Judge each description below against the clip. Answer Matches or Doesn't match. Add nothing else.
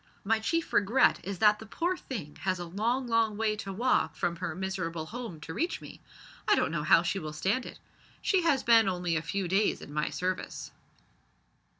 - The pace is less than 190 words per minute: Doesn't match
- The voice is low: Doesn't match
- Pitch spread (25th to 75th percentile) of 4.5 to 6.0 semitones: Matches